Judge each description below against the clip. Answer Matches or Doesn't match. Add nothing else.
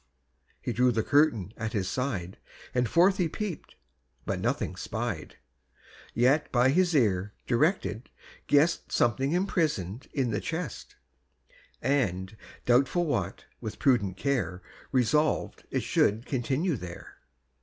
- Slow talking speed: Matches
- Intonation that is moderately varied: Doesn't match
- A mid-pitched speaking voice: Doesn't match